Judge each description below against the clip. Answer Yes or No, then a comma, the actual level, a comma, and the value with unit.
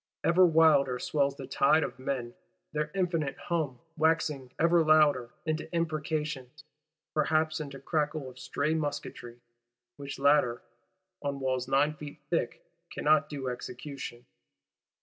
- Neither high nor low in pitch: Yes, medium, 145 Hz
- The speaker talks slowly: Yes, slow, 120 wpm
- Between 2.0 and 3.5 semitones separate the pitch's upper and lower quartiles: Yes, average, 3.2 semitones